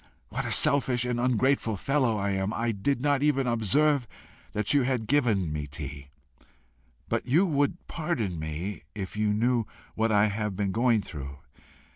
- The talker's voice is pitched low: Yes, low, 115 Hz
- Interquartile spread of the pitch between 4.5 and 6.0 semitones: Yes, average, 5.2 semitones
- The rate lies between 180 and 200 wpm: No, average, 165 wpm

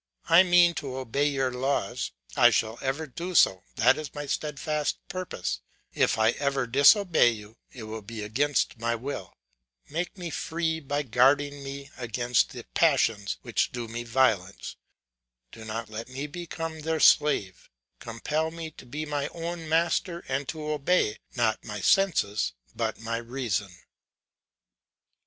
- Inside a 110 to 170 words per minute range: Yes, average, 150 wpm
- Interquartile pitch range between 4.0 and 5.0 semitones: No, wide, 5.4 semitones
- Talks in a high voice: No, low, 135 Hz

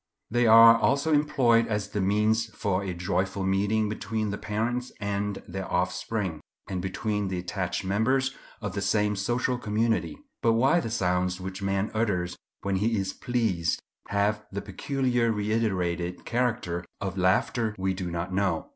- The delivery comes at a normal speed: Yes, average, 155 wpm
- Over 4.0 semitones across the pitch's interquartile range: No, average, 3.4 semitones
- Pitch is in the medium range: No, low, 105 Hz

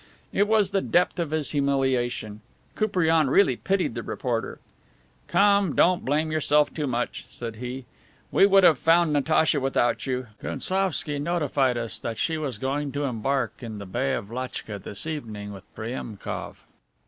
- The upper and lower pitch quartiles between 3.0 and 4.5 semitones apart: No, average, 5.2 semitones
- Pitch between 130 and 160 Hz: Yes, medium, 140 Hz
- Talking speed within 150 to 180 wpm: Yes, average, 160 wpm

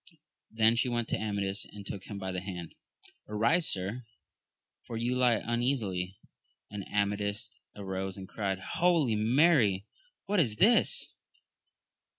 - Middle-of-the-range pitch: No, low, 105 Hz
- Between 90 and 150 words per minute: Yes, average, 145 wpm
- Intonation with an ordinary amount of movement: Yes, average, 3.8 semitones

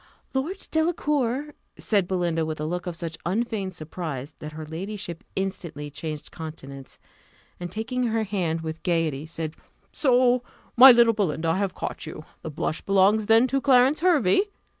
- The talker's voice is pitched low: No, medium, 185 Hz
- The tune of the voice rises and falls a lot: Yes, wide, 7.0 semitones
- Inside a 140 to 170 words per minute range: Yes, average, 160 wpm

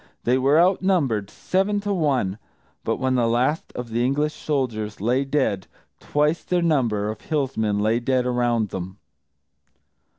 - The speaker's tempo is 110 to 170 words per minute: Yes, average, 145 wpm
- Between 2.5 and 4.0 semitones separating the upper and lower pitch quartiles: No, average, 5.2 semitones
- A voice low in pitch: Yes, low, 130 Hz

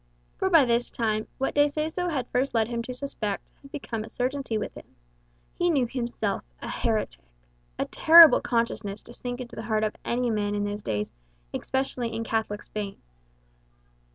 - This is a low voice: No, high, 235 Hz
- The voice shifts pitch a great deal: No, average, 3.9 semitones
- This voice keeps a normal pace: Yes, average, 180 wpm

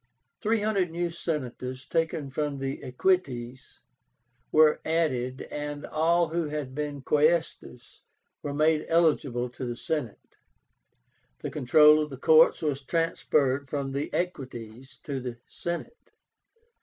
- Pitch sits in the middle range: Yes, medium, 150 Hz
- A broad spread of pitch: No, average, 3.8 semitones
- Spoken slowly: Yes, slow, 125 wpm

